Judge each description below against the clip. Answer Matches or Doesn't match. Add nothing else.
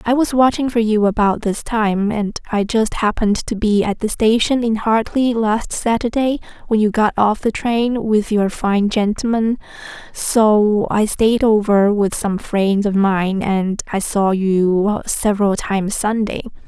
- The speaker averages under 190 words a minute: Matches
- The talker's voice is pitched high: Matches